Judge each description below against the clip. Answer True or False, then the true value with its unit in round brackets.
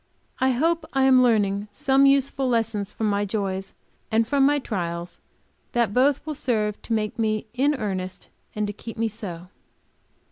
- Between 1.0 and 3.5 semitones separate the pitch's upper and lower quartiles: False (4.5 semitones)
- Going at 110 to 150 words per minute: False (175 wpm)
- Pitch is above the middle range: True (225 Hz)